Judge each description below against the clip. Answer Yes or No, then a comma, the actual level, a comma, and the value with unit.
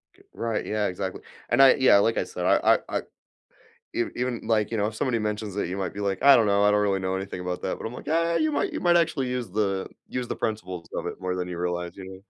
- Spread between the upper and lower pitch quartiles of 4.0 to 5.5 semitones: Yes, average, 4.4 semitones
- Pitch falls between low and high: No, low, 105 Hz